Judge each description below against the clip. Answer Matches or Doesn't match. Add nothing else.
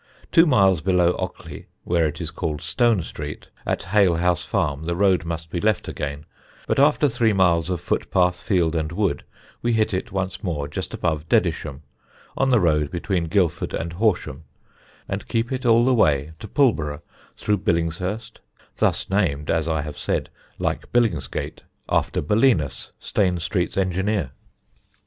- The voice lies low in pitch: Matches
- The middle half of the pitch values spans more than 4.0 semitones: Matches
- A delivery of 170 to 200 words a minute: Doesn't match